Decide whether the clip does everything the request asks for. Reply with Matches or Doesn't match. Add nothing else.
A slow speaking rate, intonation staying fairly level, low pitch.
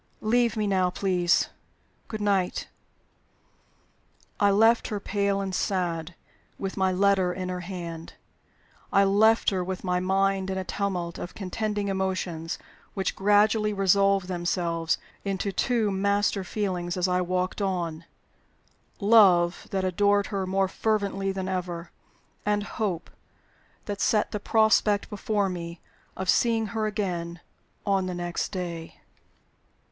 Doesn't match